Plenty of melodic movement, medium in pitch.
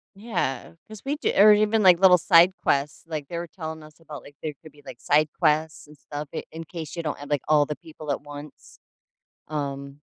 No: average, 2.9 semitones; medium, 155 Hz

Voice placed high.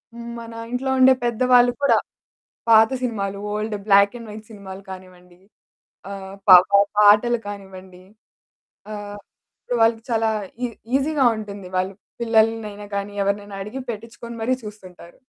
Yes: high, 210 Hz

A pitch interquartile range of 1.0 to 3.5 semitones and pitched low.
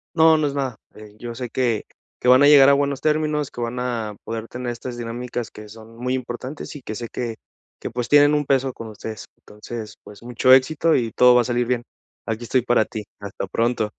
Yes: average, 2.8 semitones; low, 120 Hz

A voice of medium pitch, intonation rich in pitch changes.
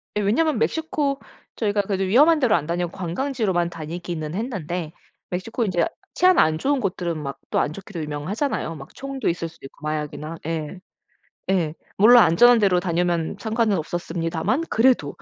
Yes: medium, 180 Hz; wide, 5.9 semitones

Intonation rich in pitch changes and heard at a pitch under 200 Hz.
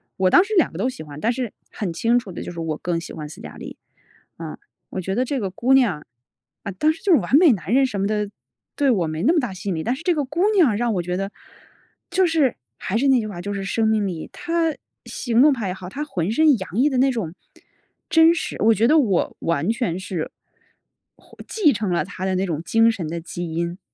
No: wide, 6.9 semitones; high, 215 Hz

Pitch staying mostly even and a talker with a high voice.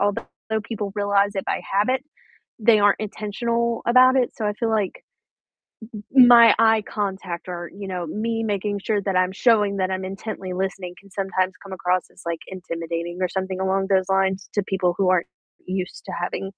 Yes: narrow, 2.3 semitones; high, 195 Hz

